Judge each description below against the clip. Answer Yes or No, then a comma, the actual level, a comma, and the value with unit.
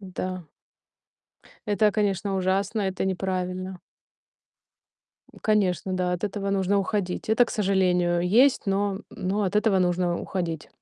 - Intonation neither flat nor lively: No, narrow, 2.0 semitones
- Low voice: No, high, 190 Hz